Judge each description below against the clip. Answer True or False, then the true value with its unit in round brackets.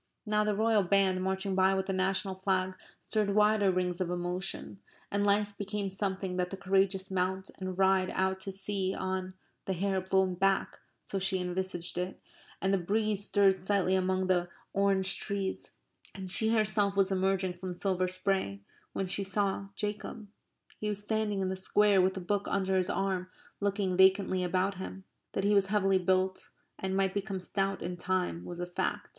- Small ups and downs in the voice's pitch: True (1.2 semitones)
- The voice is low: False (190 Hz)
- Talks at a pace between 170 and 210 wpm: True (180 wpm)